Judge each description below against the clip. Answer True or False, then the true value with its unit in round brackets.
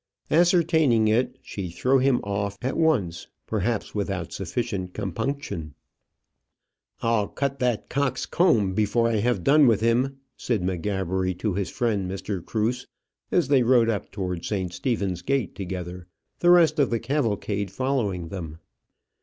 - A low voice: True (110 Hz)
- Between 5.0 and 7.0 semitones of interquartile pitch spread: True (5.4 semitones)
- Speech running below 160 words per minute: True (145 wpm)